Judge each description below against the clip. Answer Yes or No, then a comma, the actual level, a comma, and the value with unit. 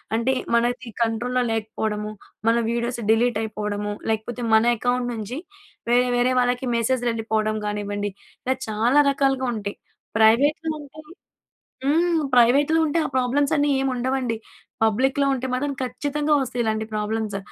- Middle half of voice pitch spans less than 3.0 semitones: No, average, 3.3 semitones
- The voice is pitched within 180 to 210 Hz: No, high, 240 Hz